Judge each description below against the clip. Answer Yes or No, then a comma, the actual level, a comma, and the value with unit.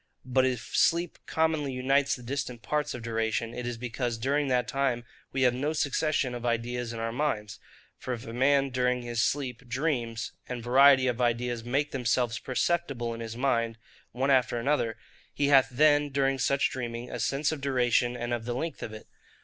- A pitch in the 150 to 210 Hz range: No, low, 125 Hz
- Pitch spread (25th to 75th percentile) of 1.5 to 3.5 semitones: Yes, average, 2.8 semitones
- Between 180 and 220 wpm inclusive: Yes, average, 190 wpm